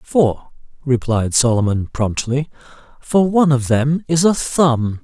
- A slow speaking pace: Yes, slow, 130 wpm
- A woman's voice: No, male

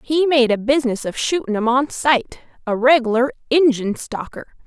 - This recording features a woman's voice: Yes, female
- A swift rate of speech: No, average, 155 wpm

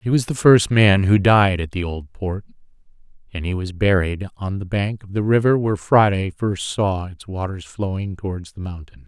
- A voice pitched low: Yes, low, 100 Hz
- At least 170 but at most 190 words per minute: No, fast, 205 wpm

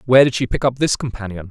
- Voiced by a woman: No, male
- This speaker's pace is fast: Yes, fast, 280 wpm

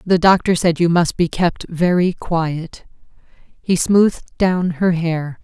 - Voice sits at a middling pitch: Yes, medium, 175 Hz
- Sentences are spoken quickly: No, average, 155 wpm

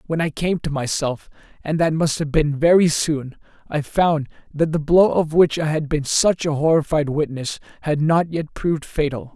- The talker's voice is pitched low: No, medium, 155 Hz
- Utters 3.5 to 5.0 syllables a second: Yes, 4.7 syllables/s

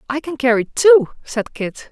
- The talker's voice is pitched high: Yes, very high, 260 Hz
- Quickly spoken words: No, average, 190 wpm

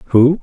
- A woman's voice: No, male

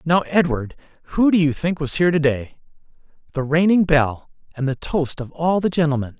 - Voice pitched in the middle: Yes, medium, 155 Hz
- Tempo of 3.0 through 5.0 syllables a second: No, 5.5 syllables/s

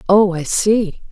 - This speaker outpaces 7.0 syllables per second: No, 3.4 syllables/s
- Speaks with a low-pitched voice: No, high, 190 Hz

